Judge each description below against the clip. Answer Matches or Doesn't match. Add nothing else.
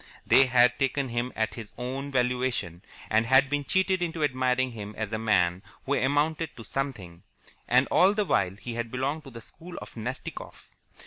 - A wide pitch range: Doesn't match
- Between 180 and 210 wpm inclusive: Matches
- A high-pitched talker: Doesn't match